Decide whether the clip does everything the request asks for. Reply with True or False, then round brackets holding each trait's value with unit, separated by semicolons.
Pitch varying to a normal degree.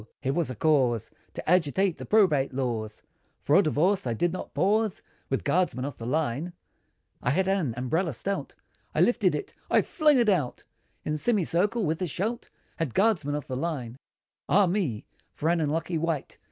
False (6.0 semitones)